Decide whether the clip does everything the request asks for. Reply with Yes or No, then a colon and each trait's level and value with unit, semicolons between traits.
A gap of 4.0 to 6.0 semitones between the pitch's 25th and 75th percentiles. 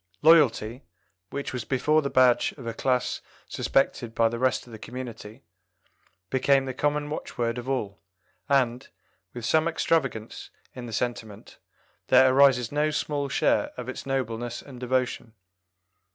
No: average, 2.8 semitones